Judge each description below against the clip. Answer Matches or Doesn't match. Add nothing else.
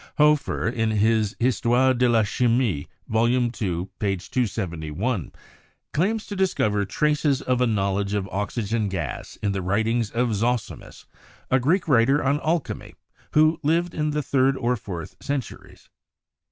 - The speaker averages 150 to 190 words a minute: Doesn't match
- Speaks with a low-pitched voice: Matches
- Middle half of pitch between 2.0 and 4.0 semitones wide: Doesn't match